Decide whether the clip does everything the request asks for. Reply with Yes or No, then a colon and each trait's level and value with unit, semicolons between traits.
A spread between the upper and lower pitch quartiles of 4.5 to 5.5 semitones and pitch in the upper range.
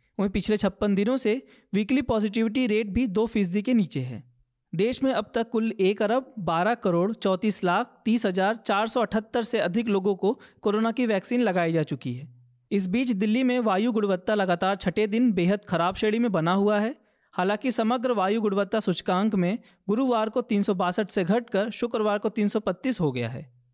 No: average, 3.3 semitones; high, 210 Hz